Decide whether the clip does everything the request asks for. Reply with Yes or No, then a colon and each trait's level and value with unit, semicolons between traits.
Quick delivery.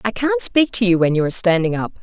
Yes: fast, 295 wpm